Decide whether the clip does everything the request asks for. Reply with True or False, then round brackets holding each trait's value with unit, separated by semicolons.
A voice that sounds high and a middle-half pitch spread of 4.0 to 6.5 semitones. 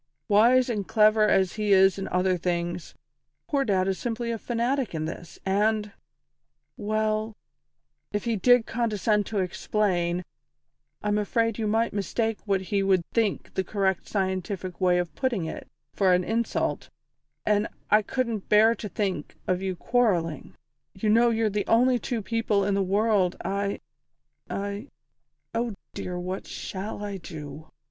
False (205 Hz; 3.0 semitones)